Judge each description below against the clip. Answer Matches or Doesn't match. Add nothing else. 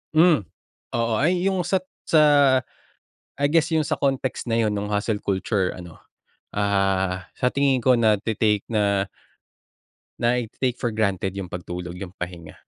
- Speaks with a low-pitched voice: Matches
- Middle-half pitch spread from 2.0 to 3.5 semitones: Doesn't match